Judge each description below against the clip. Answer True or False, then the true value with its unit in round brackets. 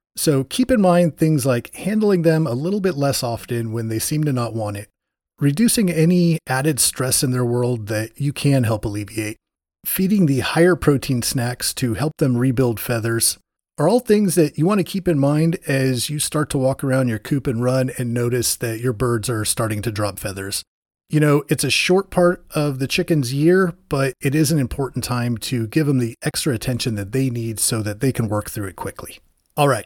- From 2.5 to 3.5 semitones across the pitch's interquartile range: False (5.0 semitones)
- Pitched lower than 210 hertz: True (135 Hz)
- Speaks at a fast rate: True (215 wpm)